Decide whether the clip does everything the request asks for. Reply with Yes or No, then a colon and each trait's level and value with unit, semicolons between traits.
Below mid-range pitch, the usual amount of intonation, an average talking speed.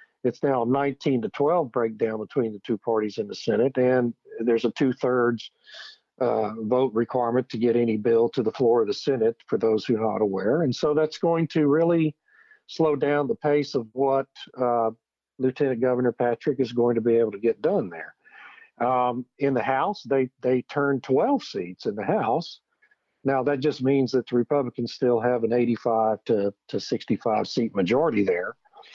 Yes: low, 125 Hz; average, 3.7 semitones; average, 190 wpm